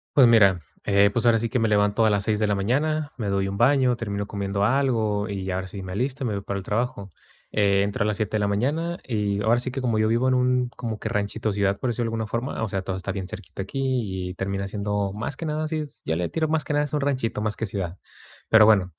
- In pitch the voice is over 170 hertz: No, low, 110 Hz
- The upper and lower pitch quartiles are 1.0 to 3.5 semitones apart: No, average, 3.9 semitones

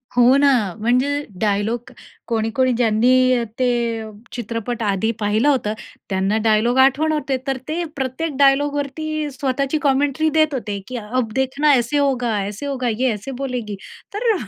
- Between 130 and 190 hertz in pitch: No, very high, 255 Hz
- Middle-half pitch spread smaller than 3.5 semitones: No, average, 3.8 semitones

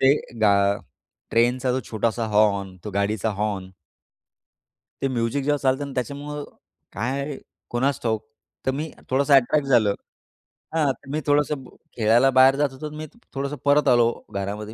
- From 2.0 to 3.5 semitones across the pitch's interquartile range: No, average, 4.5 semitones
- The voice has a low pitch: Yes, low, 130 Hz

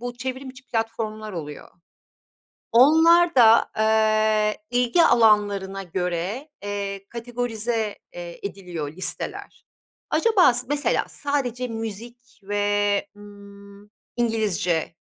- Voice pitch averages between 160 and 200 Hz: No, high, 220 Hz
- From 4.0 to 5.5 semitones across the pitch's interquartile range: No, average, 3.4 semitones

